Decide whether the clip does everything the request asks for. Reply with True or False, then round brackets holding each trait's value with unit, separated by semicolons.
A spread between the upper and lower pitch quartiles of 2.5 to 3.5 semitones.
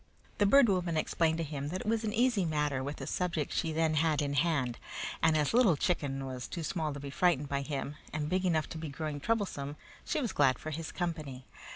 False (3.9 semitones)